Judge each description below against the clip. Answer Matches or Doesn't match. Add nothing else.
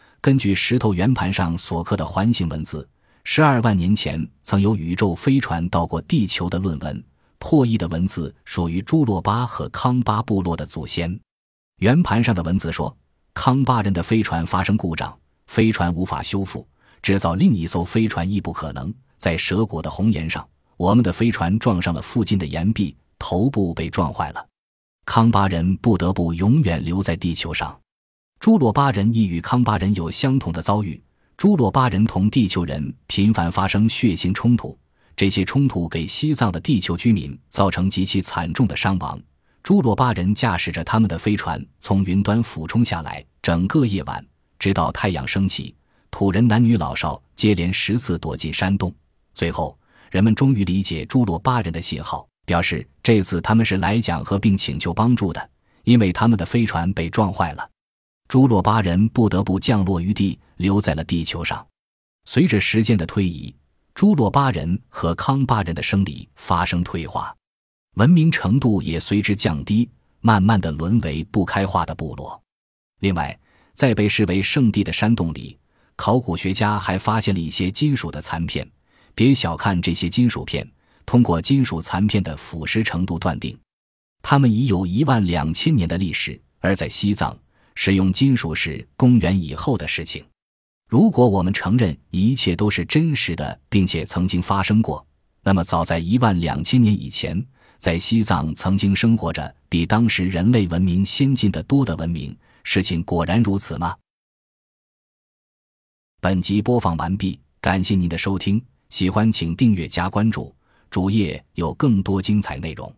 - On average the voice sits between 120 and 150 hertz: Doesn't match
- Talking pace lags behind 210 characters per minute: Doesn't match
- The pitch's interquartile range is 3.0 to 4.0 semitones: Doesn't match